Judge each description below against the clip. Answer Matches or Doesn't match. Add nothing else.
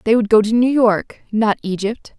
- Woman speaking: Matches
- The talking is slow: Doesn't match